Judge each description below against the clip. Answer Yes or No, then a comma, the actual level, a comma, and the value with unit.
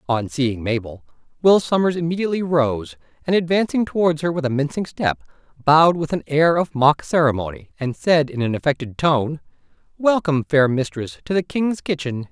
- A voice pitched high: No, medium, 150 Hz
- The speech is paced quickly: No, average, 170 wpm